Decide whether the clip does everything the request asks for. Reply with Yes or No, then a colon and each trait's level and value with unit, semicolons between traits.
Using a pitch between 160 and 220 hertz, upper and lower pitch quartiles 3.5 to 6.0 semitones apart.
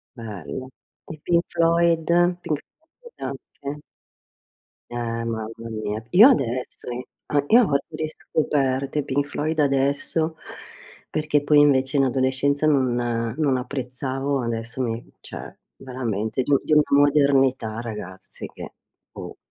No: low, 135 Hz; average, 3.8 semitones